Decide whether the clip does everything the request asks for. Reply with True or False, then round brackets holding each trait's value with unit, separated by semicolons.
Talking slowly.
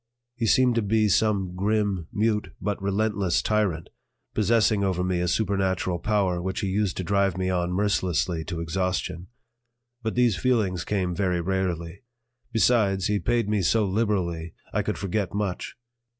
False (155 wpm)